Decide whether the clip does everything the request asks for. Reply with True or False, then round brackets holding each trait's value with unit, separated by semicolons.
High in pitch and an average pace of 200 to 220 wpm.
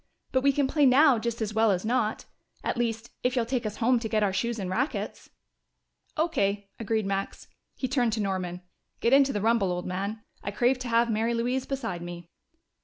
True (230 Hz; 205 wpm)